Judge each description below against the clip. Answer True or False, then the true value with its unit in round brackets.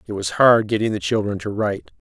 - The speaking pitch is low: True (105 Hz)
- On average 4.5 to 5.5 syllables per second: False (6.0 syllables/s)